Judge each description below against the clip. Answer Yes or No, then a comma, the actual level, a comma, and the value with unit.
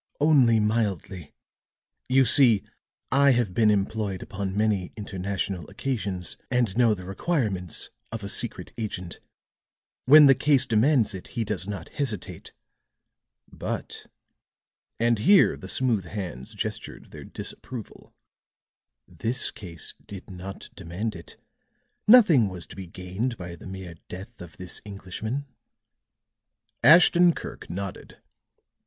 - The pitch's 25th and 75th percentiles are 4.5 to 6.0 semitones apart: Yes, average, 4.8 semitones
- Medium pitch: No, low, 105 Hz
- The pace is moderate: No, slow, 125 wpm